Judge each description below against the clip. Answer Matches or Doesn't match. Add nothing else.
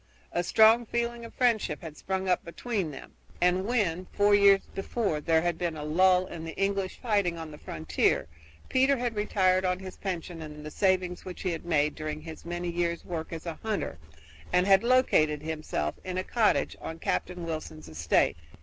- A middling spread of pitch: Matches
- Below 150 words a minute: Doesn't match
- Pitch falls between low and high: Matches